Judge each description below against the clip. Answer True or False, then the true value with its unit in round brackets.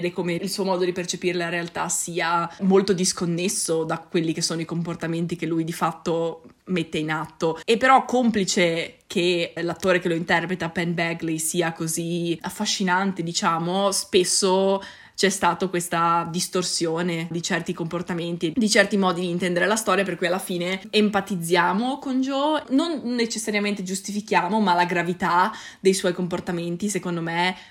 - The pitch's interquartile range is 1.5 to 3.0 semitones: True (2.4 semitones)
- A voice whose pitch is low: False (180 Hz)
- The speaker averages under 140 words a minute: False (155 wpm)